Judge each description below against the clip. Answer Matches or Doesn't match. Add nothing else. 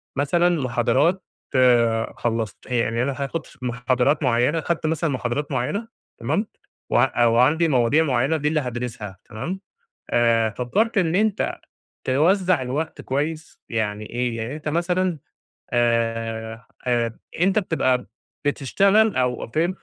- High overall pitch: Doesn't match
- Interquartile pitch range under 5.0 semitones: Doesn't match